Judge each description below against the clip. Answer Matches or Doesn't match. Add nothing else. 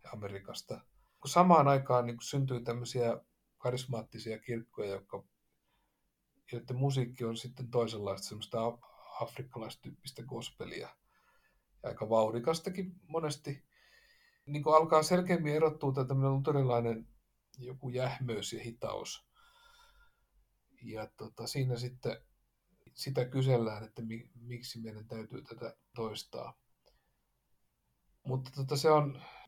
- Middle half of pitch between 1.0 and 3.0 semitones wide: Doesn't match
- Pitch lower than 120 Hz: Doesn't match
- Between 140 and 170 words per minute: Doesn't match